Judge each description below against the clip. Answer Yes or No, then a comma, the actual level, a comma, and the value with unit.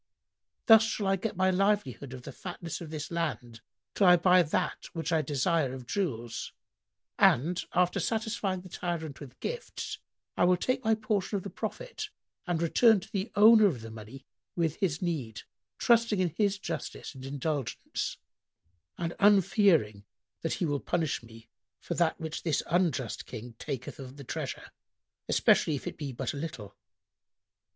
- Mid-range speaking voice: Yes, medium, 165 Hz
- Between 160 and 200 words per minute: Yes, average, 165 wpm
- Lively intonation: Yes, wide, 6.2 semitones